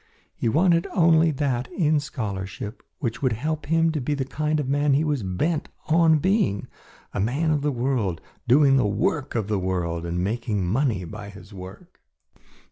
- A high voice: No, low, 135 Hz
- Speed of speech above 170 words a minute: Yes, average, 180 wpm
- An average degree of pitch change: No, wide, 7.0 semitones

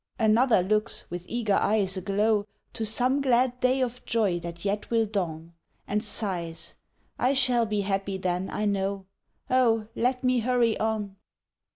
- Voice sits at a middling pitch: No, high, 215 Hz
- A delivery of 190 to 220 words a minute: No, average, 155 wpm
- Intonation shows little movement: No, average, 3.8 semitones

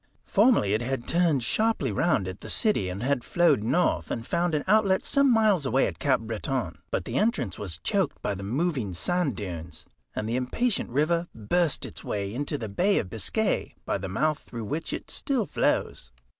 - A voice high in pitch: No, low, 135 Hz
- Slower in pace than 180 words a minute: No, average, 195 wpm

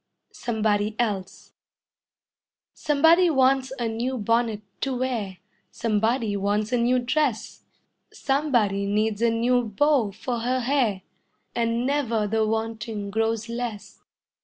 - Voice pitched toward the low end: No, high, 230 Hz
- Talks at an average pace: No, slow, 115 wpm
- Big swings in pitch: No, average, 3.1 semitones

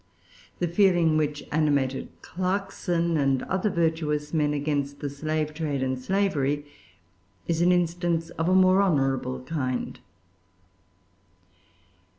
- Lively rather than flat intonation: No, average, 3.5 semitones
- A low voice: No, medium, 155 Hz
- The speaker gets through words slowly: Yes, slow, 115 wpm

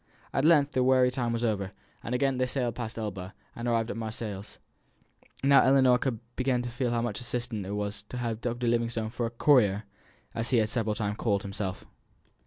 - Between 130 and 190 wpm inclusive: No, fast, 205 wpm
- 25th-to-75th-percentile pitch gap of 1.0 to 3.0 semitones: Yes, average, 2.7 semitones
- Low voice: Yes, low, 115 Hz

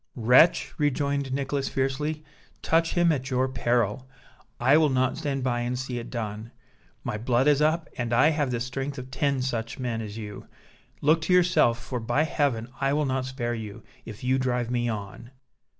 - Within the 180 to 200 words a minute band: Yes, average, 185 wpm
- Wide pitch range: No, average, 3.0 semitones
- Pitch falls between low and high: No, low, 130 Hz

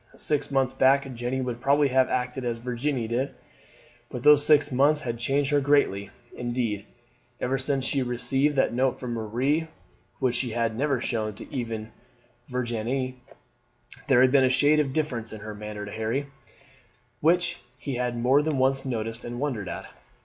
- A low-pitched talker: Yes, low, 130 Hz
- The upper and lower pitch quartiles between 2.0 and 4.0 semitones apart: Yes, average, 2.9 semitones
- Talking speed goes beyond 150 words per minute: Yes, average, 170 wpm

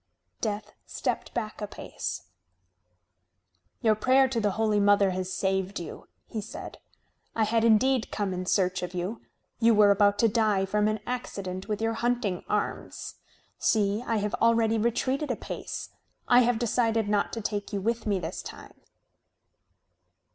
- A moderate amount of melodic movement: No, narrow, 2.3 semitones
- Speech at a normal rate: Yes, average, 160 wpm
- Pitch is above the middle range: Yes, high, 215 Hz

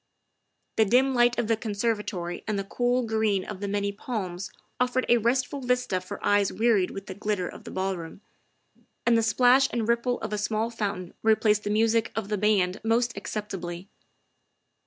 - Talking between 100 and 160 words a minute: No, average, 175 wpm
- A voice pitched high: Yes, high, 215 Hz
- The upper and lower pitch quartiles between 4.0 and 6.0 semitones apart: No, average, 3.1 semitones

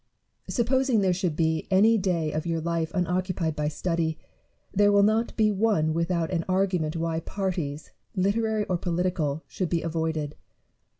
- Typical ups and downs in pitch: Yes, average, 3.6 semitones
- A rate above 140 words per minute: Yes, average, 155 wpm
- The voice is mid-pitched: Yes, medium, 175 Hz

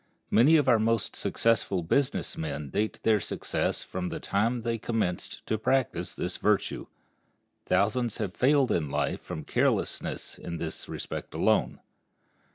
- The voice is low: Yes, low, 110 Hz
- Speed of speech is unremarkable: Yes, average, 145 wpm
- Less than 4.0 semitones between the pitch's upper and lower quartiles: No, average, 5.3 semitones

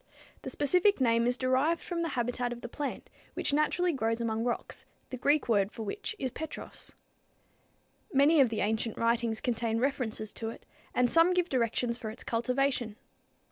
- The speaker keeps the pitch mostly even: No, average, 3.9 semitones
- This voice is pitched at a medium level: No, high, 245 Hz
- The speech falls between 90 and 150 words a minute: No, average, 175 wpm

